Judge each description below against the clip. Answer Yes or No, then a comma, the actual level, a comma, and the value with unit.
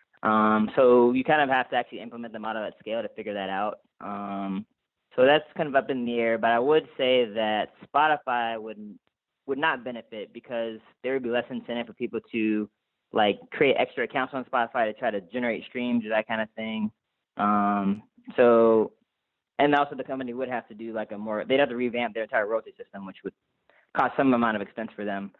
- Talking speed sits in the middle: No, fast, 215 wpm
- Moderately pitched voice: No, low, 115 Hz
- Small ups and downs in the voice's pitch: No, average, 3.0 semitones